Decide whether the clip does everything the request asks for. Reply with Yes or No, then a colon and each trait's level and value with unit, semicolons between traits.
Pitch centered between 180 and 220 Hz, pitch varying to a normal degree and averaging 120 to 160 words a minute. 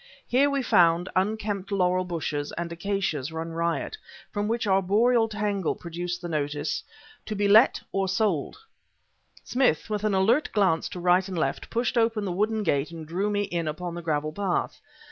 No: high, 190 Hz; average, 3.9 semitones; average, 175 wpm